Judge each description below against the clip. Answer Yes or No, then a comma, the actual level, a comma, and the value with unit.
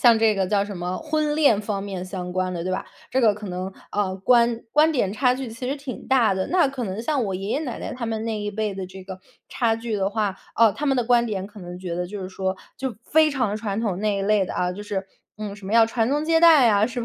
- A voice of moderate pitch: No, high, 215 Hz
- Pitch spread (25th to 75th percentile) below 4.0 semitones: No, average, 4.4 semitones